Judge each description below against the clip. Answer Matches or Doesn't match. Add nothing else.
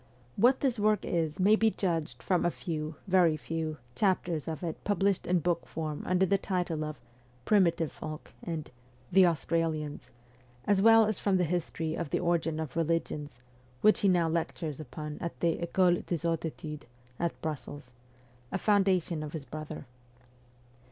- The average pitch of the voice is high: Doesn't match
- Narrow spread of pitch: Doesn't match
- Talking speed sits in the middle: Matches